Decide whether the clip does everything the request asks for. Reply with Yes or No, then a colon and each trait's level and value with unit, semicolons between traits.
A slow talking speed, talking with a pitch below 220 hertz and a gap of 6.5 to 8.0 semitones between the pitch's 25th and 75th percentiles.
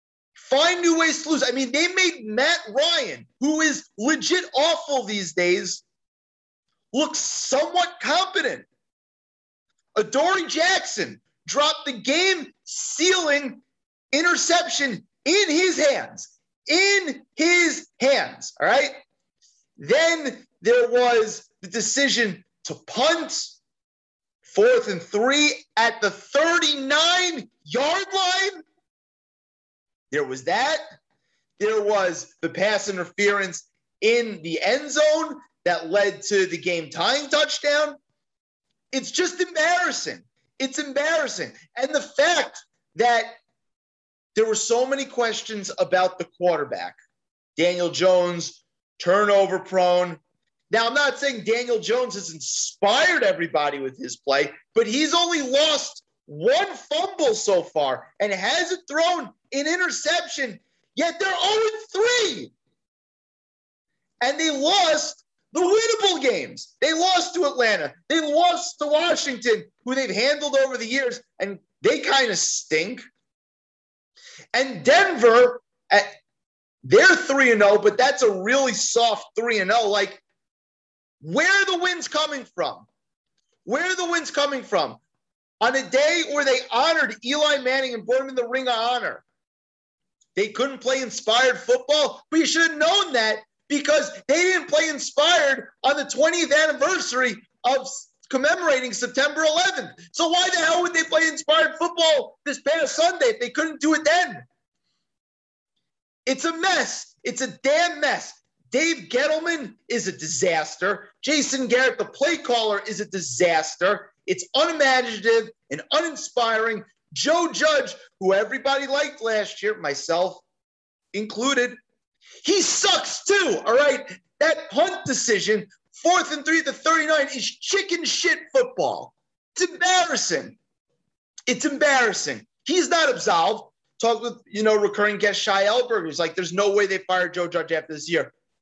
No: slow, 130 wpm; very high, 275 Hz; wide, 7.0 semitones